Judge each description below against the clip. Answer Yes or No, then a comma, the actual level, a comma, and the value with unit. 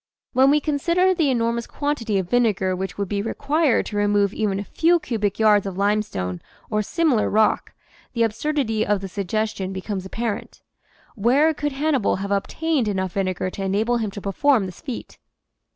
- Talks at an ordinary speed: Yes, average, 180 wpm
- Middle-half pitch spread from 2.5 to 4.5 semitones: No, average, 5.3 semitones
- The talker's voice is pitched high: Yes, high, 215 Hz